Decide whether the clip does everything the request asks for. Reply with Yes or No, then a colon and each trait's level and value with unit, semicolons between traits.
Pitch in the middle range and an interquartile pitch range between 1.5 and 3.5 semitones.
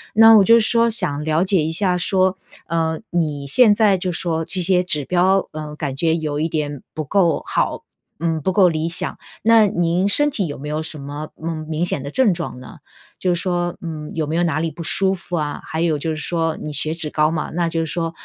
Yes: medium, 165 Hz; average, 3.1 semitones